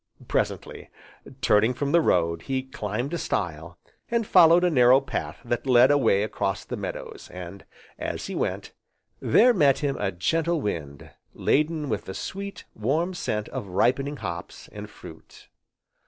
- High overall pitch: No, low, 130 Hz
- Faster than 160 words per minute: No, average, 155 wpm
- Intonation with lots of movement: Yes, wide, 7.7 semitones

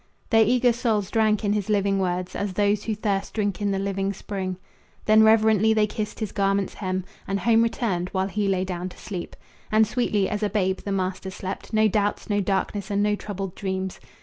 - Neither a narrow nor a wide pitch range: No, narrow, 2.1 semitones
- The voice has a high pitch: Yes, high, 200 Hz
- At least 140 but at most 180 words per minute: No, fast, 205 wpm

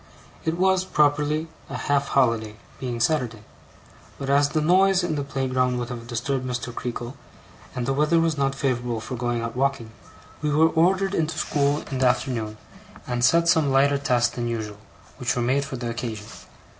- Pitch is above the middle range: No, low, 135 Hz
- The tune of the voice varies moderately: Yes, average, 3.8 semitones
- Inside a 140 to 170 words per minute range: No, average, 180 wpm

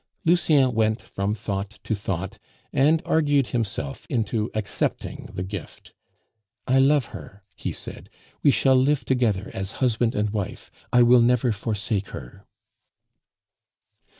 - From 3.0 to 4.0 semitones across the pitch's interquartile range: No, average, 4.5 semitones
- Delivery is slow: Yes, slow, 130 wpm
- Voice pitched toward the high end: No, low, 115 Hz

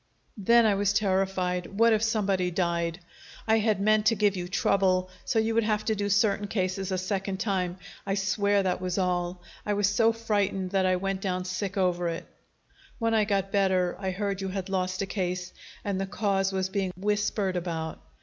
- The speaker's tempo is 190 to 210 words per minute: Yes, average, 195 wpm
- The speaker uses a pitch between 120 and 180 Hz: No, high, 195 Hz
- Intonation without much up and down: Yes, narrow, 2.0 semitones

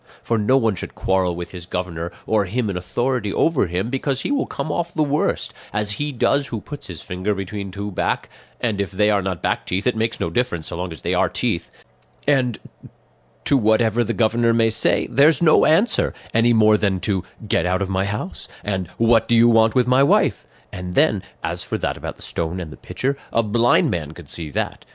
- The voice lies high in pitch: No, low, 105 Hz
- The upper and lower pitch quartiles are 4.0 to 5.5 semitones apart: Yes, average, 4.7 semitones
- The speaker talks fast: Yes, fast, 220 wpm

